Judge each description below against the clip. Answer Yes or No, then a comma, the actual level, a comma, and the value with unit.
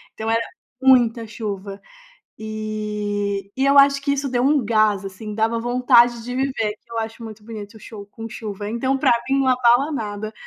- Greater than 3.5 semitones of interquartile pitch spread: No, average, 3.0 semitones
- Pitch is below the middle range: No, high, 225 Hz